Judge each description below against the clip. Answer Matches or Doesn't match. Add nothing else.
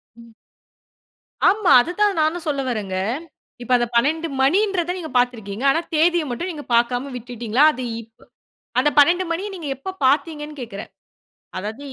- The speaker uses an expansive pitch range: Matches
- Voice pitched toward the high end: Matches